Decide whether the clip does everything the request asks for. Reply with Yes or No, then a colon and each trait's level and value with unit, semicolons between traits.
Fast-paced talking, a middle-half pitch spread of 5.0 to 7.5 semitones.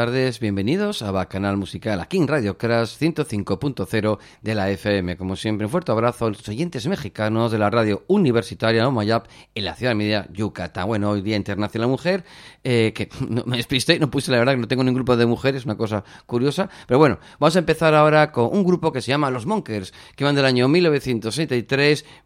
Yes: fast, 215 wpm; average, 5.3 semitones